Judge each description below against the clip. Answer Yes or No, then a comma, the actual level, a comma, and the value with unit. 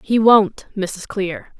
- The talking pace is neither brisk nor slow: Yes, average, 150 wpm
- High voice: Yes, high, 205 Hz